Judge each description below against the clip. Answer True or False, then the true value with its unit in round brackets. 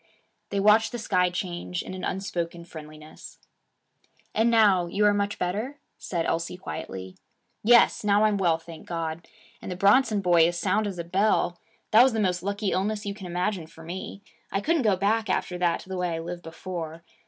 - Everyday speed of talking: True (195 wpm)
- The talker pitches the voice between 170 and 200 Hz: True (185 Hz)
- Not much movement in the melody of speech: False (3.3 semitones)